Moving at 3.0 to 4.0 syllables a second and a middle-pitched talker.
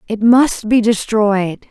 No: 3.3 syllables/s; high, 220 Hz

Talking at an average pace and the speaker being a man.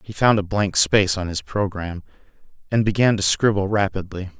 Yes: average, 175 wpm; male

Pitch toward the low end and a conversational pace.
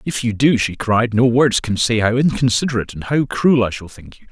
No: low, 120 Hz; fast, 250 wpm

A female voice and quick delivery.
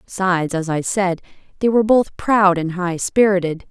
No: female; average, 180 wpm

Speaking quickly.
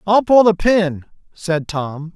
No: average, 165 wpm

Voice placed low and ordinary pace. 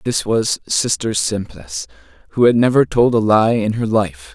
Yes: low, 105 Hz; average, 180 wpm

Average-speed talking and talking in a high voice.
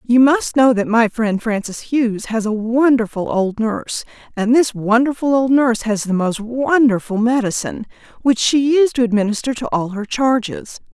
Yes: average, 175 wpm; high, 235 Hz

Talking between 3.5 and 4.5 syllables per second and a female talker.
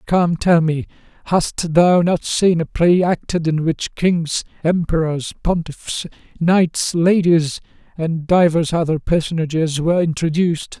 No: 4.0 syllables/s; male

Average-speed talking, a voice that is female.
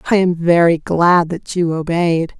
Yes: average, 175 wpm; female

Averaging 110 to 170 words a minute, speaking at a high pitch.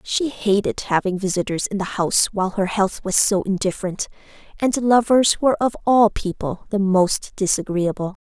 Yes: average, 160 wpm; high, 200 Hz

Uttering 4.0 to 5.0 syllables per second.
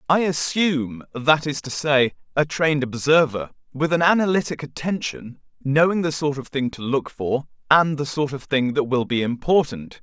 Yes: 4.9 syllables/s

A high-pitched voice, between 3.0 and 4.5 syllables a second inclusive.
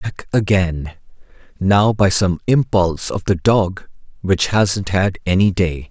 No: very low, 95 Hz; 3.8 syllables/s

